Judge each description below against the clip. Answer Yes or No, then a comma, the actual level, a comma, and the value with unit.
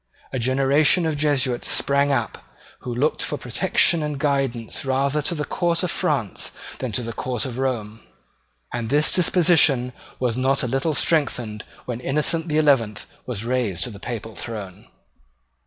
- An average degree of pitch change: Yes, average, 3.9 semitones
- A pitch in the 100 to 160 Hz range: Yes, low, 135 Hz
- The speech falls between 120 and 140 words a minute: No, average, 160 wpm